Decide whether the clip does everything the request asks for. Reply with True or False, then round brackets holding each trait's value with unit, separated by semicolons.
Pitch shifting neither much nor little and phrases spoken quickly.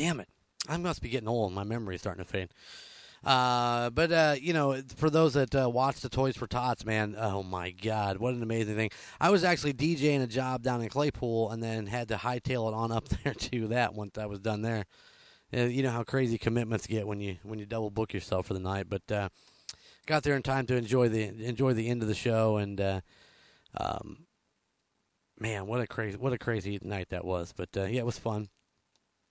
True (3.8 semitones; 230 wpm)